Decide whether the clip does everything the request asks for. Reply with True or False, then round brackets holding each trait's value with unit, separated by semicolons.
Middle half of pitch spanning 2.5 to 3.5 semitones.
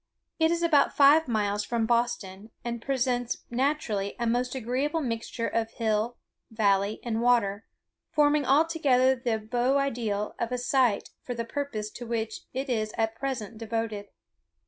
True (3.2 semitones)